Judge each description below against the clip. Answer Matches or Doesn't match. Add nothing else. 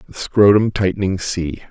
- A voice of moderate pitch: Doesn't match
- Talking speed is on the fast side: Doesn't match